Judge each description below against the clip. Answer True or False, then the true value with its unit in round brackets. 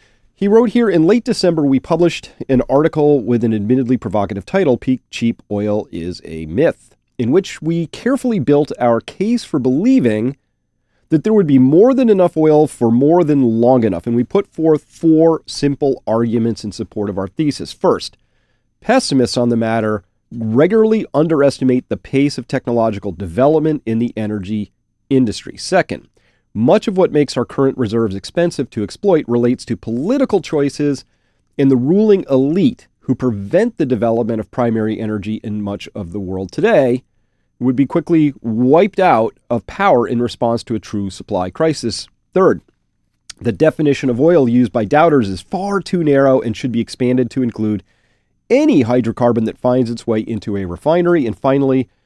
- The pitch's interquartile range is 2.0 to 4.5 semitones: False (5.3 semitones)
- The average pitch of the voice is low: True (125 Hz)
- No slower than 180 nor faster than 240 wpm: False (170 wpm)